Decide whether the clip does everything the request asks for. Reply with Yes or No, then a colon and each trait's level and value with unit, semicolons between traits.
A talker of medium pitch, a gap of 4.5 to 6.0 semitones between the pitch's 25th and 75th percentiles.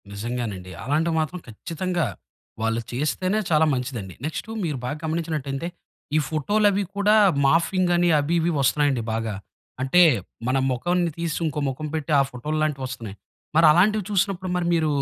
Yes: medium, 155 Hz; average, 5.1 semitones